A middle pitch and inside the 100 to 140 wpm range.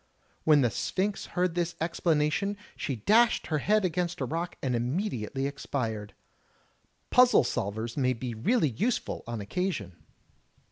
Yes: medium, 150 Hz; slow, 135 wpm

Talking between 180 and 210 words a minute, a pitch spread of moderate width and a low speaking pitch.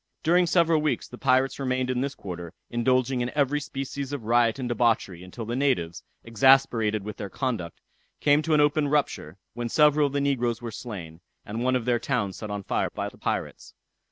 Yes: average, 200 wpm; average, 4.3 semitones; low, 125 Hz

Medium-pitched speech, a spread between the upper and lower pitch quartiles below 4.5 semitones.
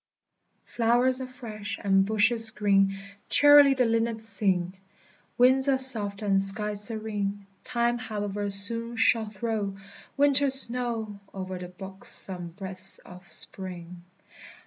No: high, 215 Hz; average, 3.3 semitones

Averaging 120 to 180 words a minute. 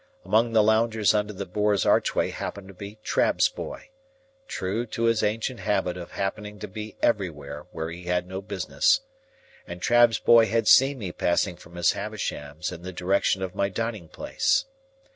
Yes: average, 165 wpm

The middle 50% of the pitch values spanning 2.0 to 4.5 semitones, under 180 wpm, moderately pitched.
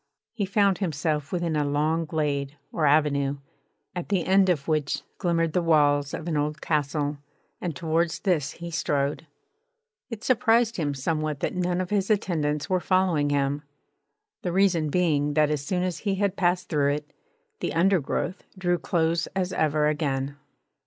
Yes: average, 3.6 semitones; average, 165 wpm; medium, 160 Hz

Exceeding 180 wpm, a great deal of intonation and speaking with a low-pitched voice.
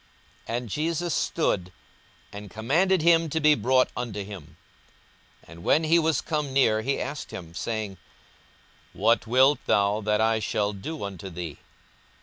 No: average, 155 wpm; wide, 6.9 semitones; low, 115 Hz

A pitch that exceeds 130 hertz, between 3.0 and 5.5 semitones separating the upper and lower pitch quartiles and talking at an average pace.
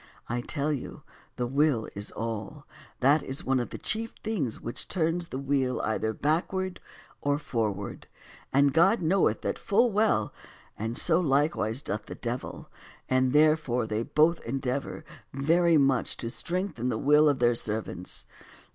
Yes: medium, 140 Hz; average, 5.1 semitones; average, 155 wpm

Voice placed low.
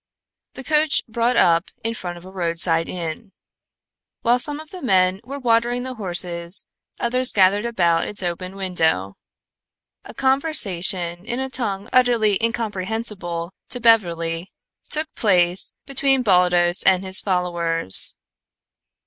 No: high, 195 Hz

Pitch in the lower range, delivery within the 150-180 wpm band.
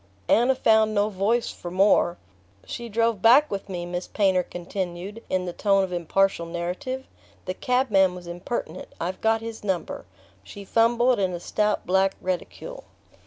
No: high, 195 Hz; average, 160 wpm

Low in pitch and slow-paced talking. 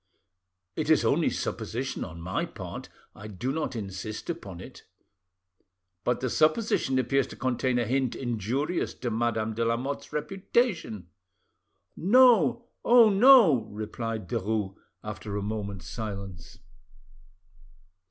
Yes: low, 120 Hz; slow, 120 wpm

